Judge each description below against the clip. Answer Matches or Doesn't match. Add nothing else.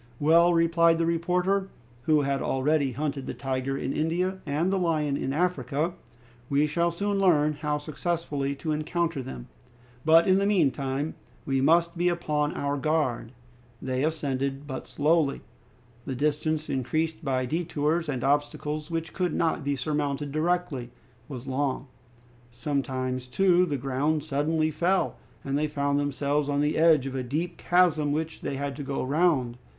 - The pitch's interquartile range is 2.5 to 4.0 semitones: Matches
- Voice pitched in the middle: Matches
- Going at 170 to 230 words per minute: Doesn't match